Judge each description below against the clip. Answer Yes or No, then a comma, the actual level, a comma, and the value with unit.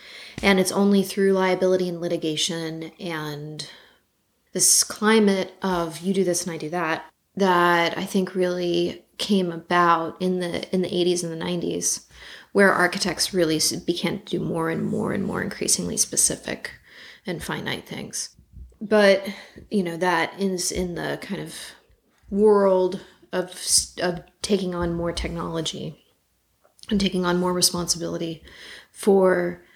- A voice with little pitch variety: Yes, narrow, 1.9 semitones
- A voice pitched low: No, medium, 180 Hz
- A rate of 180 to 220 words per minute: No, average, 140 wpm